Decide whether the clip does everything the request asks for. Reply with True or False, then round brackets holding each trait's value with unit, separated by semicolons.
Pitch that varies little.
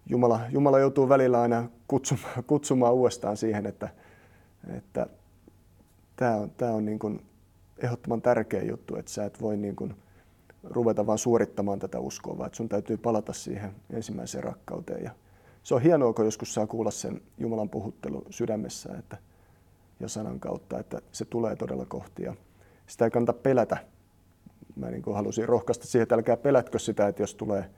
False (3.3 semitones)